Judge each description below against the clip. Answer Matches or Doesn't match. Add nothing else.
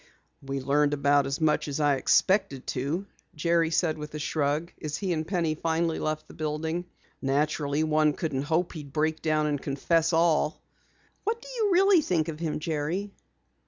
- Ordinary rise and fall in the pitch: Doesn't match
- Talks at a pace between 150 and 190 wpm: Matches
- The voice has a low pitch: Doesn't match